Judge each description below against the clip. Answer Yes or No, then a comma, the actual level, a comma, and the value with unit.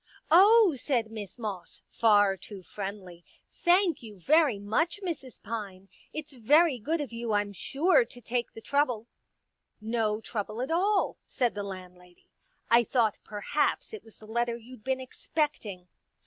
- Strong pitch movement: Yes, wide, 6.2 semitones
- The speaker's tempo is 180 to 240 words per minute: No, average, 170 wpm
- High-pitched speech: Yes, high, 230 Hz